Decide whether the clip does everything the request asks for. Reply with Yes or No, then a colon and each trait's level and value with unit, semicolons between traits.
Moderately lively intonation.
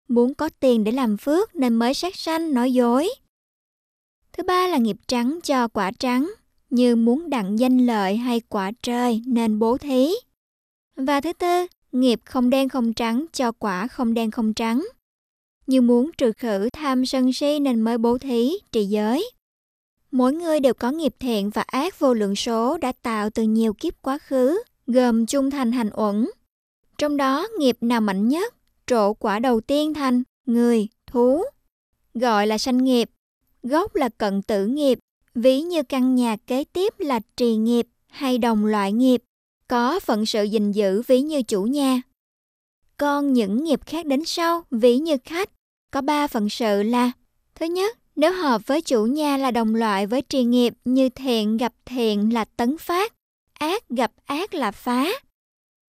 Yes: average, 3.7 semitones